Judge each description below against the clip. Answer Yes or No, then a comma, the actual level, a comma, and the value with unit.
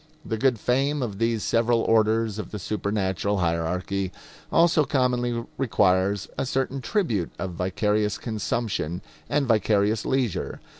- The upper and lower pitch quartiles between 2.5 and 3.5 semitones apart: No, average, 3.9 semitones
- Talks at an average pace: No, slow, 130 wpm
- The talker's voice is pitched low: Yes, low, 110 Hz